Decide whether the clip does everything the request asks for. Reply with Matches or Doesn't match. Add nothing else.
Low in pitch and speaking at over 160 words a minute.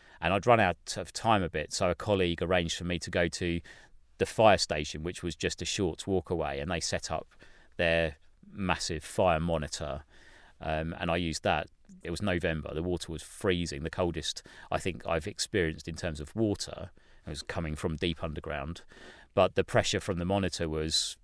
Matches